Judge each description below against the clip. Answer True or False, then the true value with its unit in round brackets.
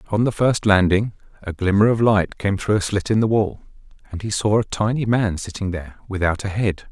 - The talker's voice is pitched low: True (100 Hz)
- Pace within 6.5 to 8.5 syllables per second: False (5.5 syllables/s)